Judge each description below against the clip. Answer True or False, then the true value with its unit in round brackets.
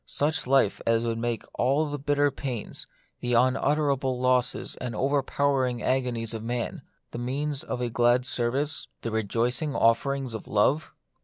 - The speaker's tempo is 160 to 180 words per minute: False (150 wpm)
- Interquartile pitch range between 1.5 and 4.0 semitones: True (2.9 semitones)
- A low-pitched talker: True (125 Hz)